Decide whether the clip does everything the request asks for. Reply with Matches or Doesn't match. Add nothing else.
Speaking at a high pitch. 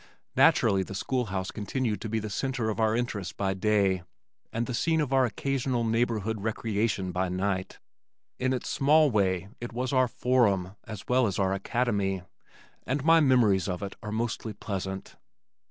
Doesn't match